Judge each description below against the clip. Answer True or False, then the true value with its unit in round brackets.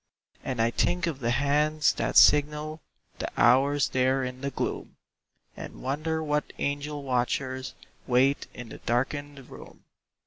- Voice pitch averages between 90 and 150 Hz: True (140 Hz)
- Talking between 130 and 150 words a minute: True (140 wpm)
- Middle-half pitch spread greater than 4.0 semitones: False (2.5 semitones)